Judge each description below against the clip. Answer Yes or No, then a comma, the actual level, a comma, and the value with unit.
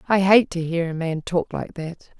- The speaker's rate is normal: No, fast, 245 wpm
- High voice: No, medium, 175 Hz